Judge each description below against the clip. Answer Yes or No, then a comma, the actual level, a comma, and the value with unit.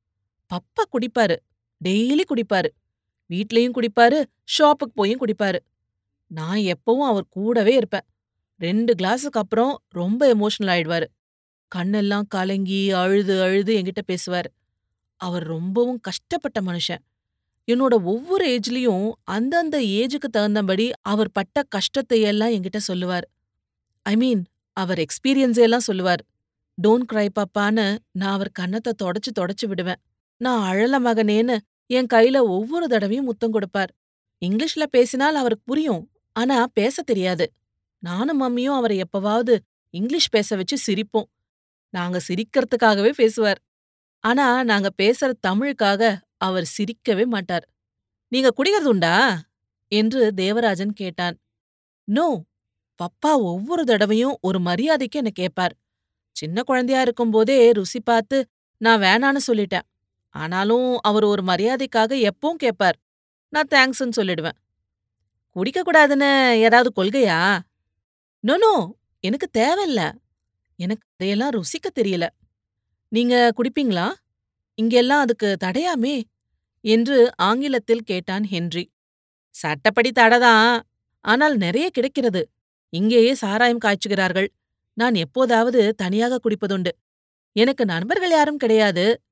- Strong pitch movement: No, average, 4.9 semitones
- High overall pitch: Yes, high, 215 Hz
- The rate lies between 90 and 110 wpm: Yes, average, 105 wpm